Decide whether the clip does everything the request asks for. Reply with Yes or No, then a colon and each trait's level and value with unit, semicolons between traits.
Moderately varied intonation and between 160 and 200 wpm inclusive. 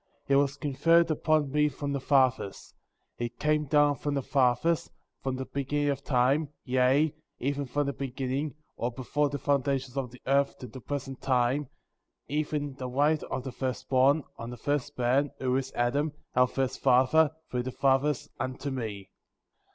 No: narrow, 2.2 semitones; average, 180 wpm